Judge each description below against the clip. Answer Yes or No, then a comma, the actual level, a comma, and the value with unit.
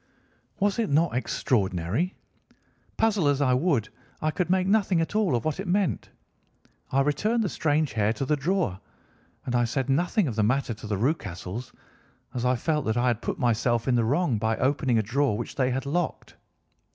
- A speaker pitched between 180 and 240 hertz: No, low, 135 Hz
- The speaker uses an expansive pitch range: Yes, wide, 6.4 semitones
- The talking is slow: No, average, 195 wpm